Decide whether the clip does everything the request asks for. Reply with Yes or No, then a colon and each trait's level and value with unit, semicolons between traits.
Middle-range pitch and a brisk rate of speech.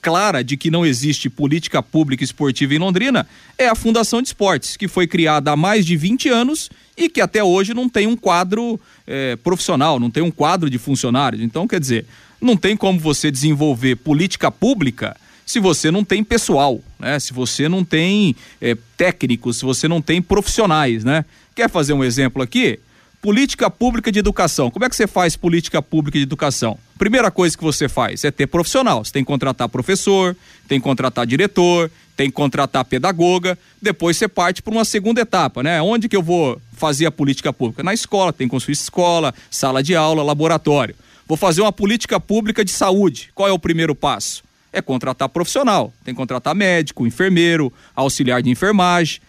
Yes: medium, 165 Hz; fast, 190 wpm